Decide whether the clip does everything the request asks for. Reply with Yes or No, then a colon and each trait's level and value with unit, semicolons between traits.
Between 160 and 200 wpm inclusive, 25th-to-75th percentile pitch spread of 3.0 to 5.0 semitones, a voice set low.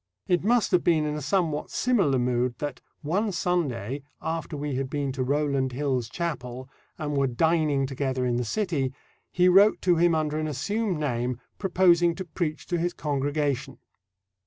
No: average, 170 wpm; average, 4.7 semitones; medium, 150 Hz